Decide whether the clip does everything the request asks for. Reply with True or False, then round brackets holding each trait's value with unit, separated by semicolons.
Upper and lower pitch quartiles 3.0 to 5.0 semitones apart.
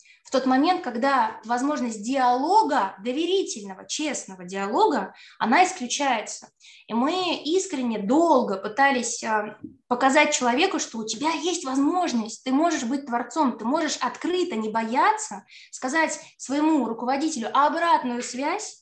True (4.7 semitones)